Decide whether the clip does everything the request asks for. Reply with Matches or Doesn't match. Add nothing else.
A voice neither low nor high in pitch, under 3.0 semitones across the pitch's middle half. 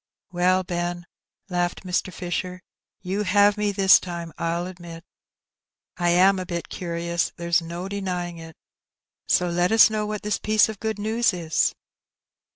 Matches